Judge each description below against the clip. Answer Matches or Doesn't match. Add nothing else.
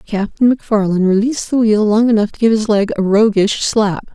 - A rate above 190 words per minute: Matches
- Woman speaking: Matches